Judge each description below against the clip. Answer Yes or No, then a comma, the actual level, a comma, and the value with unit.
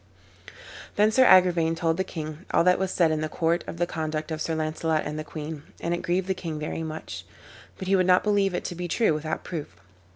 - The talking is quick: Yes, fast, 235 wpm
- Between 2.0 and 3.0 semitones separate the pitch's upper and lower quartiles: Yes, narrow, 2.6 semitones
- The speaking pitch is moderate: Yes, medium, 165 Hz